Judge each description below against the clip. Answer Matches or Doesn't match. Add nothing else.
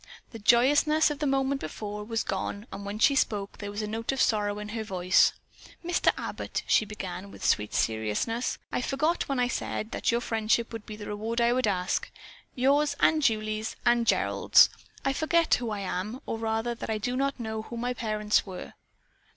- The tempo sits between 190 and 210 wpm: Matches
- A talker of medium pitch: Doesn't match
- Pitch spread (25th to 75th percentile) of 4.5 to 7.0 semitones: Doesn't match